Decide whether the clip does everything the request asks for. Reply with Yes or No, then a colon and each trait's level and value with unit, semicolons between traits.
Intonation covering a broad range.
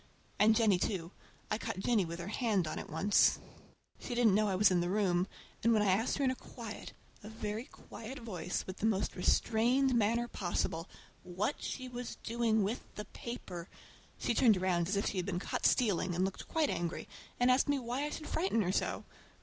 No: average, 4.3 semitones